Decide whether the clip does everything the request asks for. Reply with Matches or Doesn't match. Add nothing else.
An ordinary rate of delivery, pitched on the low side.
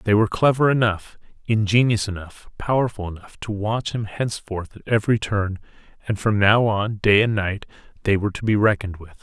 Matches